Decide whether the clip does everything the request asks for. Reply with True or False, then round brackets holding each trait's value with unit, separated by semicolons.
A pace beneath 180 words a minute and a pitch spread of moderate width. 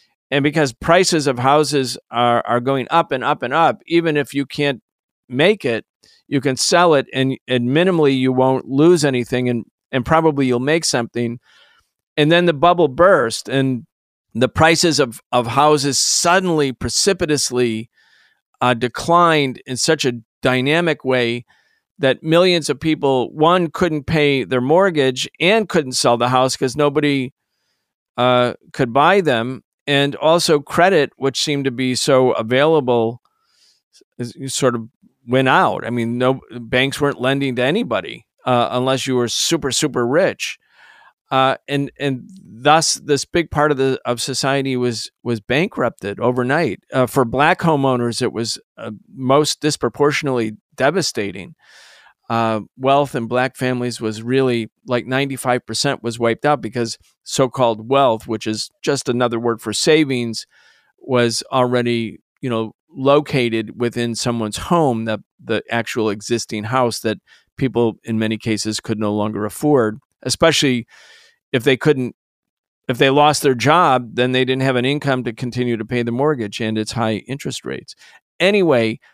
True (150 wpm; 3.6 semitones)